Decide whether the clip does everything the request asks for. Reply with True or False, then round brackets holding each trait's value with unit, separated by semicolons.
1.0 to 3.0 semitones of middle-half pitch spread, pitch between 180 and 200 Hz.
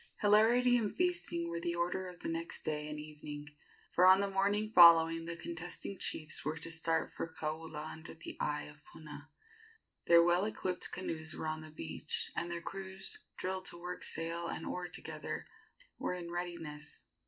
False (2.7 semitones; 170 Hz)